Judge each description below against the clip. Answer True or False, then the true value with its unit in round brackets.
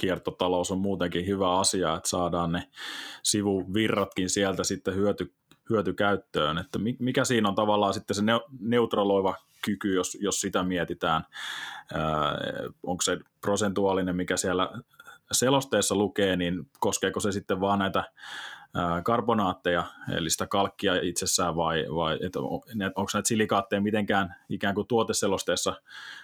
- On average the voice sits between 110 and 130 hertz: False (100 Hz)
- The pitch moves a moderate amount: False (2.3 semitones)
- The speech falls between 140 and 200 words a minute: False (130 wpm)